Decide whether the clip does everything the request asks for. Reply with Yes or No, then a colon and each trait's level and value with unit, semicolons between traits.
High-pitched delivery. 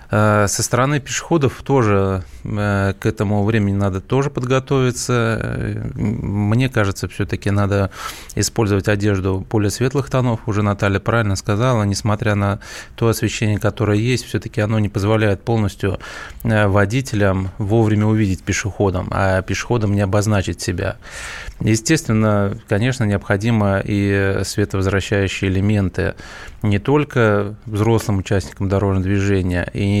No: low, 105 Hz